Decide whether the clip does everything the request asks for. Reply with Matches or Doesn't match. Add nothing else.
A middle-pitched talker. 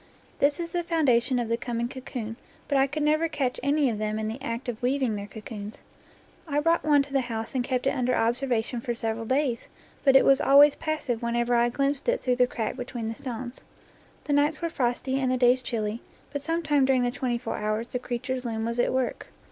Doesn't match